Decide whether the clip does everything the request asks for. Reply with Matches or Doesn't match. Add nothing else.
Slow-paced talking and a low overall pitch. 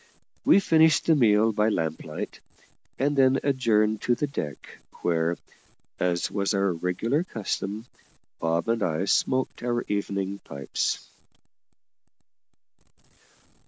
Matches